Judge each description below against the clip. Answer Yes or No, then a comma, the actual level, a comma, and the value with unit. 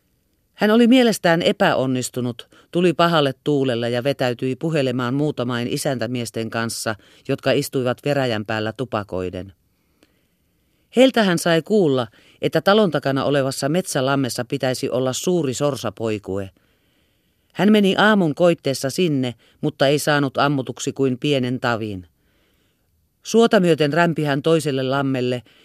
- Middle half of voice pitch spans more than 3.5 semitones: Yes, average, 4.6 semitones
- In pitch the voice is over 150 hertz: No, low, 135 Hz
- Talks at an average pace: Yes, average, 115 wpm